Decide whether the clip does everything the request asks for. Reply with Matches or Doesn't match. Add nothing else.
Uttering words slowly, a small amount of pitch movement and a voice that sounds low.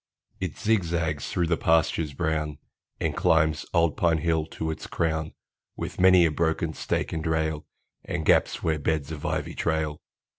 Doesn't match